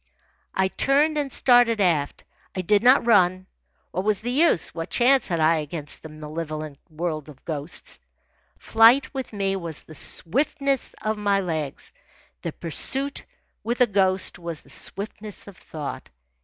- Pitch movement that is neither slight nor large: No, wide, 7.0 semitones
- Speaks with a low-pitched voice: No, high, 190 Hz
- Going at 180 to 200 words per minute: No, average, 155 wpm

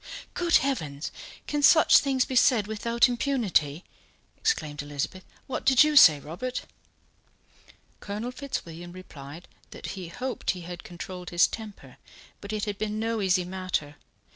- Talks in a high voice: Yes, high, 200 Hz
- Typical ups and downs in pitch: No, wide, 6.5 semitones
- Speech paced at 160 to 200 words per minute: No, average, 140 wpm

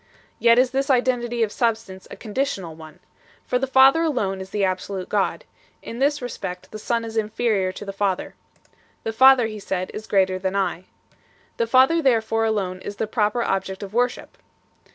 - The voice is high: Yes, high, 220 Hz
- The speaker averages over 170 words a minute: Yes, average, 180 wpm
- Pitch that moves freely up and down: No, average, 4.3 semitones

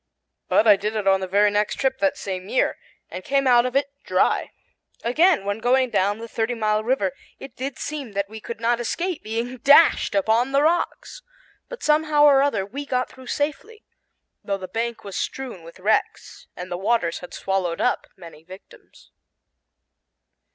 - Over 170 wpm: Yes, average, 180 wpm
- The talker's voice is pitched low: No, high, 230 Hz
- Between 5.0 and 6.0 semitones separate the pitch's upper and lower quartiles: Yes, wide, 5.4 semitones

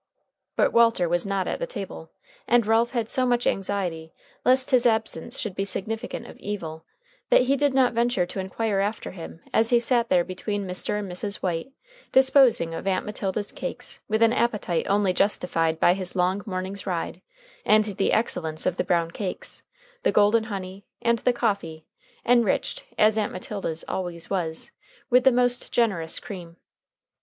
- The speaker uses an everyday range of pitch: Yes, average, 4.3 semitones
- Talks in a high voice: Yes, high, 200 Hz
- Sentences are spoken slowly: No, average, 170 wpm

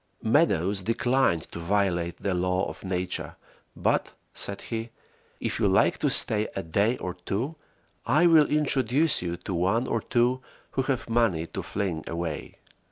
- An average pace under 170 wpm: Yes, average, 160 wpm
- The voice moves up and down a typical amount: No, wide, 5.7 semitones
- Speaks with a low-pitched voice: Yes, low, 100 Hz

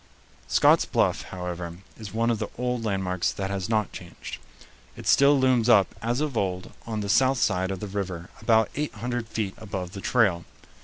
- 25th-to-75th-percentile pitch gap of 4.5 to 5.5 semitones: No, average, 4.1 semitones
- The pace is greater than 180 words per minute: Yes, average, 190 wpm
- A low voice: Yes, low, 105 Hz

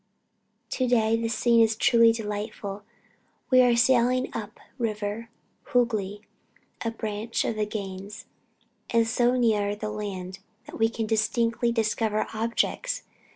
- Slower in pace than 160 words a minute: Yes, slow, 135 wpm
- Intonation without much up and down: Yes, narrow, 1.9 semitones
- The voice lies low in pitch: No, high, 225 Hz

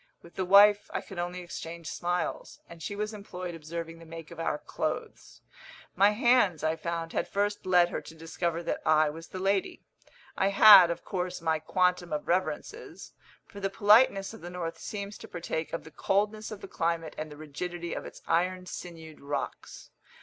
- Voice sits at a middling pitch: Yes, medium, 175 Hz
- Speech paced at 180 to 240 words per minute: Yes, average, 190 wpm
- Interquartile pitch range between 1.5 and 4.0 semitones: Yes, average, 3.1 semitones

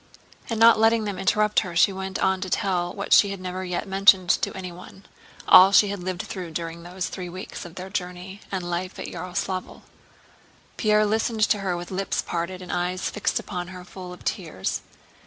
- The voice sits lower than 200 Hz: Yes, medium, 185 Hz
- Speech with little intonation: Yes, narrow, 1.8 semitones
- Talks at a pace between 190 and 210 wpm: Yes, average, 195 wpm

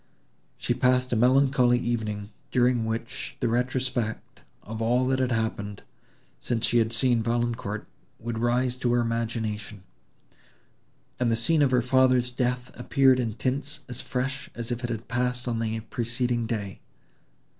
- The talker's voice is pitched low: Yes, low, 120 Hz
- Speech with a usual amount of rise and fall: No, narrow, 1.8 semitones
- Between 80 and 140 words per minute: No, average, 155 wpm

